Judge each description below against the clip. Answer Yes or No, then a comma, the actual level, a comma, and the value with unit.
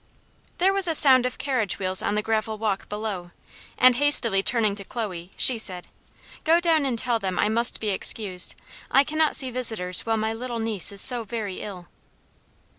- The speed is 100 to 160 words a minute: No, average, 190 wpm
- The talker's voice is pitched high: Yes, high, 225 Hz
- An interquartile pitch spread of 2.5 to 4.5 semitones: Yes, average, 4.2 semitones